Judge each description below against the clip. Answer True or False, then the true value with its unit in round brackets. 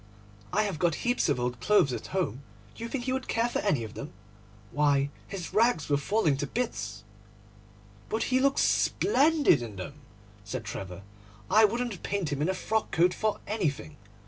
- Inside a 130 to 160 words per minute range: False (180 wpm)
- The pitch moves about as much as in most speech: False (8.5 semitones)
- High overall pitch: False (170 Hz)